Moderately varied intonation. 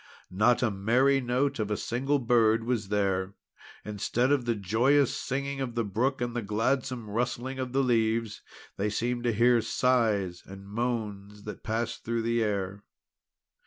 Yes: average, 3.1 semitones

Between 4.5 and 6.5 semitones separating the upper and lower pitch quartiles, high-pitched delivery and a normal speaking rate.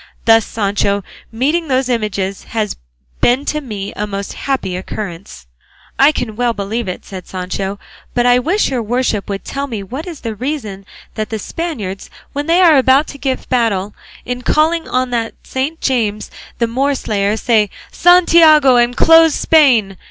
Yes: wide, 5.4 semitones; high, 240 Hz; average, 165 wpm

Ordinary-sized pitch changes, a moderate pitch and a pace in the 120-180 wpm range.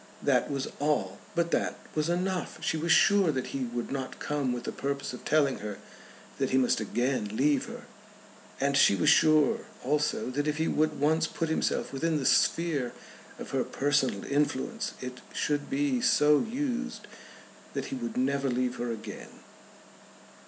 Yes: average, 4.2 semitones; medium, 145 Hz; average, 170 wpm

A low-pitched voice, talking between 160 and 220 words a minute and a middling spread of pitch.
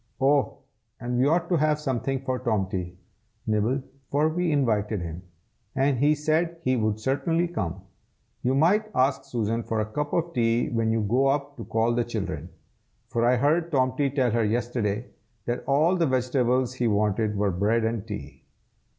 Yes: low, 125 Hz; average, 175 wpm; average, 4.4 semitones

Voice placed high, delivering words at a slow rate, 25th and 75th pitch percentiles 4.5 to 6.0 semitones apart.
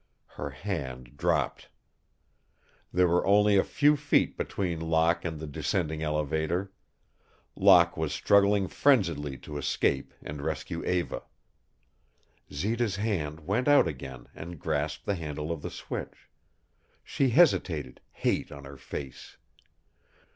No: very low, 85 Hz; slow, 125 wpm; average, 5.2 semitones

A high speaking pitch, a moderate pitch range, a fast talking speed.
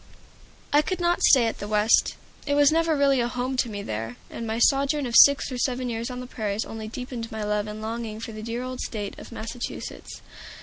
Yes: high, 235 Hz; average, 3.4 semitones; fast, 220 wpm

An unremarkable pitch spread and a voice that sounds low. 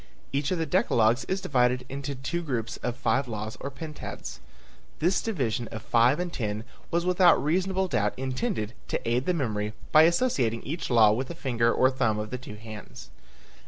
No: wide, 6.3 semitones; low, 130 Hz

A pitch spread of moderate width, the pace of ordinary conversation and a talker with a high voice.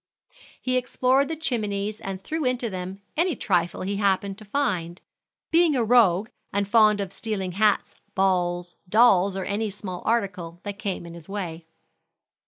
Yes: average, 4.0 semitones; average, 160 wpm; high, 200 Hz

